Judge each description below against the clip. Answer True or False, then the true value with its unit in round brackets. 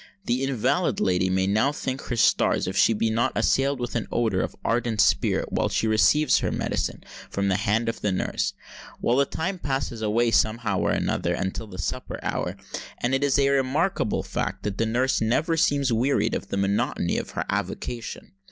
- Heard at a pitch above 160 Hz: False (115 Hz)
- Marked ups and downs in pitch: False (4.2 semitones)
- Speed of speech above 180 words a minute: True (195 wpm)